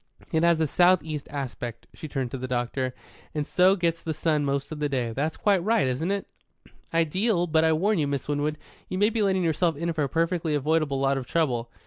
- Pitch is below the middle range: No, medium, 155 Hz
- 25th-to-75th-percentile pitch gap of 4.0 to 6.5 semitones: No, average, 3.6 semitones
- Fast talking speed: Yes, fast, 225 wpm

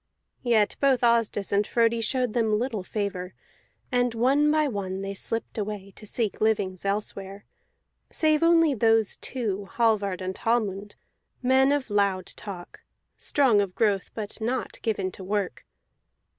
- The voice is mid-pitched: No, high, 215 Hz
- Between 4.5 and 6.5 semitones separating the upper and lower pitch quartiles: No, average, 3.5 semitones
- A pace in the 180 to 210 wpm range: No, average, 145 wpm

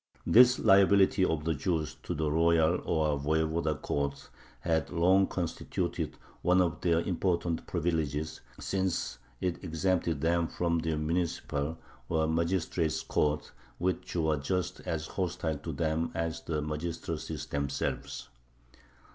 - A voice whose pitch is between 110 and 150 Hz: No, very low, 80 Hz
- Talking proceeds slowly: Yes, slow, 125 wpm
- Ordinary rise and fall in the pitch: No, narrow, 2.1 semitones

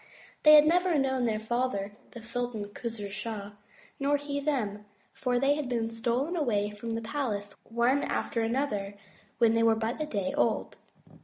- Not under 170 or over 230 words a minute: Yes, average, 175 wpm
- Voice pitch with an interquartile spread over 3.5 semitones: Yes, average, 4.4 semitones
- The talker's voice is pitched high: Yes, high, 235 Hz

